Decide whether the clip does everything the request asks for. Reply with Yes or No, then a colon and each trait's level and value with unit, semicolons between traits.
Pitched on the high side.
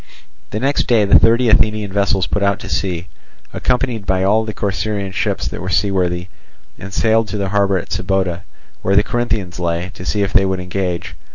No: low, 100 Hz